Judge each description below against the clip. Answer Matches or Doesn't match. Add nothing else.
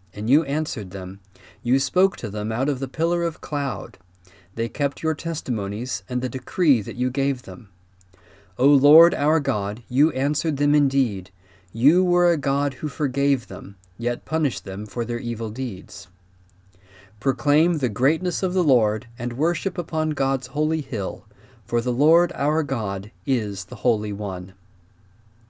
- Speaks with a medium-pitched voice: Doesn't match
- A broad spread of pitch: Matches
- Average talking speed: Matches